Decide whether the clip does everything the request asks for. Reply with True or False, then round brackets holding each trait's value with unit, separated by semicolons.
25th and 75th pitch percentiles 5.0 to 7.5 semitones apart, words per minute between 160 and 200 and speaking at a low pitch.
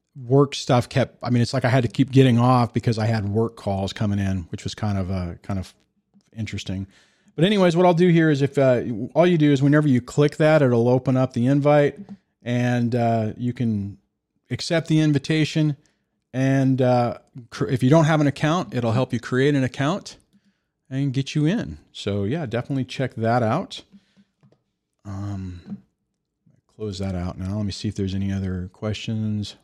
True (5.5 semitones; 195 wpm; 125 Hz)